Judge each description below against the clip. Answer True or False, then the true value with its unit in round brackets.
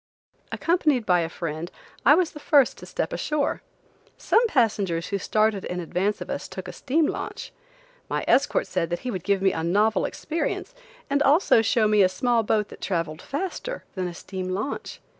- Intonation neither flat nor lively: False (7.6 semitones)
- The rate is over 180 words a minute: True (190 wpm)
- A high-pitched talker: True (210 Hz)